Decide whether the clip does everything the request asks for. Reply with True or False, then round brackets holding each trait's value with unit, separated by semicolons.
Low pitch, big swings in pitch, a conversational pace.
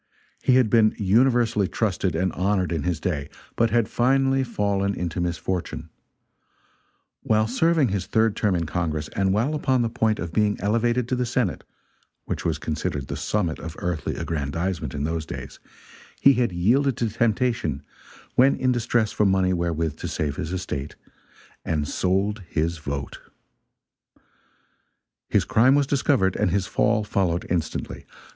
True (100 Hz; 5.9 semitones; 155 wpm)